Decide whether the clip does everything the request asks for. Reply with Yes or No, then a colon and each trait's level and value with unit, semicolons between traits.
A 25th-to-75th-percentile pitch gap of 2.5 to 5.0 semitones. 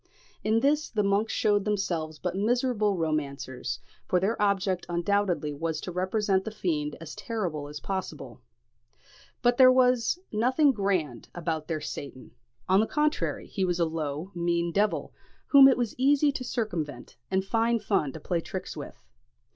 No: wide, 5.5 semitones